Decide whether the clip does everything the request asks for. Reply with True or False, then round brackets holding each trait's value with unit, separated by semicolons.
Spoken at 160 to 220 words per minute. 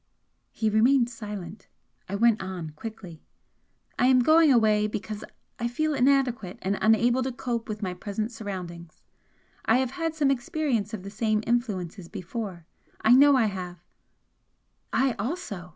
False (150 wpm)